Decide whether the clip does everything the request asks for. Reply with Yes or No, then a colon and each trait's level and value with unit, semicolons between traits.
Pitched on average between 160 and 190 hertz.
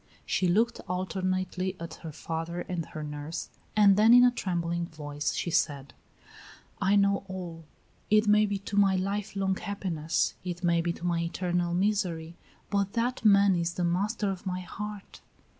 Yes: medium, 185 Hz